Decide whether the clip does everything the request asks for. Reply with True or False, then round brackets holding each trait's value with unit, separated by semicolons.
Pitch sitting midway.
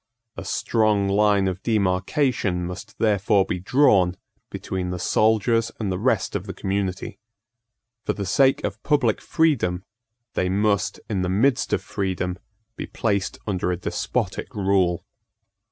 False (100 Hz)